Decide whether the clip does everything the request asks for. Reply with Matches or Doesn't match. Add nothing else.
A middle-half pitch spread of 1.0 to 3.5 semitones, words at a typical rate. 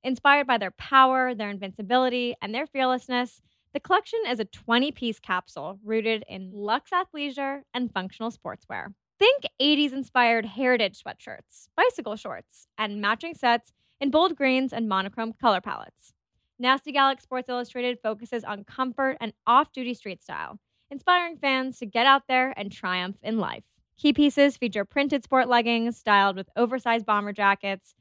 Doesn't match